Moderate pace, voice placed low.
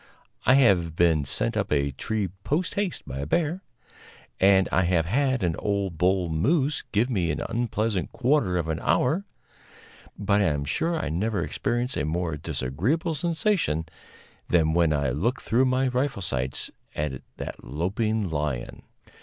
Yes: average, 160 wpm; very low, 95 Hz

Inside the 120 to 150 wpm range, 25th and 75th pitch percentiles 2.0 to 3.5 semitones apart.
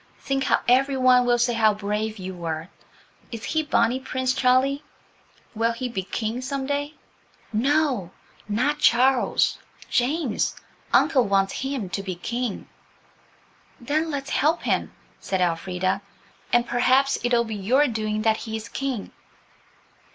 No: slow, 135 wpm; average, 4.2 semitones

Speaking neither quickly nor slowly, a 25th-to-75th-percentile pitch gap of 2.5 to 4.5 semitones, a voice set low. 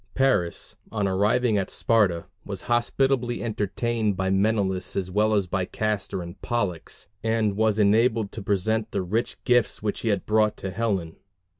Yes: average, 160 wpm; average, 2.8 semitones; low, 105 Hz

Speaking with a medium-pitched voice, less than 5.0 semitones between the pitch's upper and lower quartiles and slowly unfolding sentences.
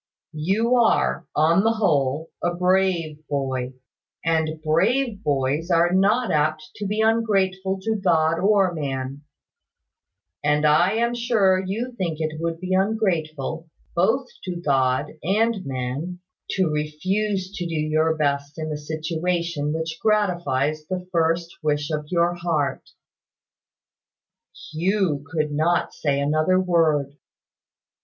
Yes: medium, 165 Hz; average, 4.0 semitones; slow, 125 wpm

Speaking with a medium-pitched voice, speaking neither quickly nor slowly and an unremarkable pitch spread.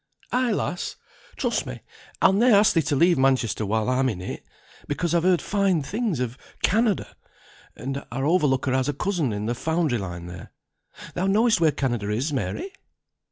No: medium, 145 Hz; average, 175 wpm; wide, 7.1 semitones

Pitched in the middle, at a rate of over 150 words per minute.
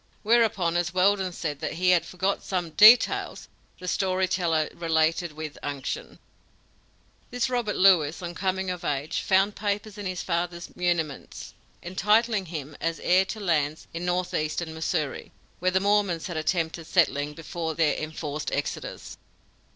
No: medium, 175 Hz; average, 145 wpm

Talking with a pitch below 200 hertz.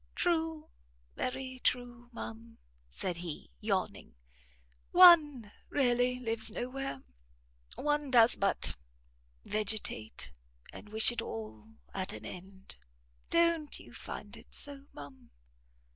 No: high, 240 Hz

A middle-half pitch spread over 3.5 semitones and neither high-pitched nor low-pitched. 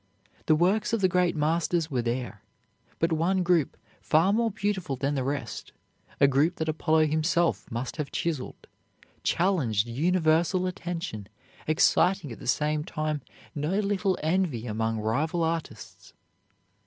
Yes: average, 4.7 semitones; medium, 160 Hz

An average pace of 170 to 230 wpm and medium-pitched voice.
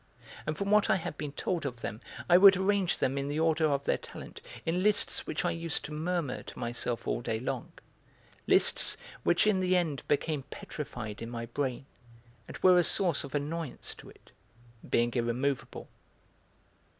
Yes: average, 180 wpm; medium, 150 Hz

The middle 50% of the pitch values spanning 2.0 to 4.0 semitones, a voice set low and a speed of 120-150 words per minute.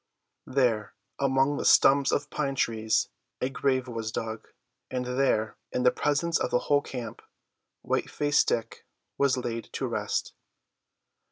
Yes: average, 3.3 semitones; low, 130 Hz; average, 145 wpm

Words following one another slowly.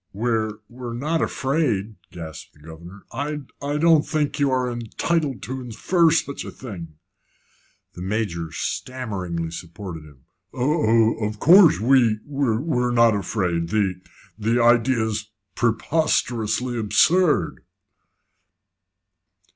Yes: slow, 115 wpm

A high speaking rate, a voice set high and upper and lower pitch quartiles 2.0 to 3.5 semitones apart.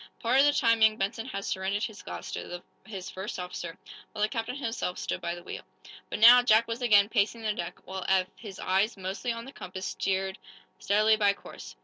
Yes: fast, 215 wpm; high, 210 Hz; average, 3.2 semitones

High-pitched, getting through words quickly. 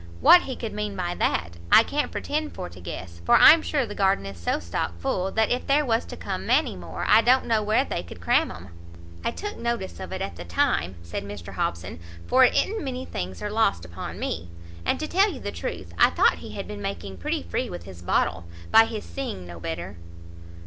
No: medium, 175 Hz; fast, 230 wpm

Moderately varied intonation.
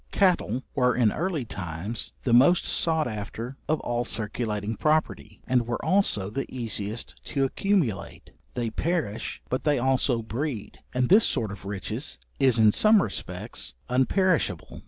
No: wide, 5.9 semitones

